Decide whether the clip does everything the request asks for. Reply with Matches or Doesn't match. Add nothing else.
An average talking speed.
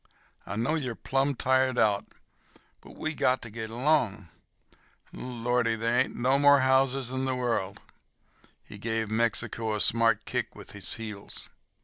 Matches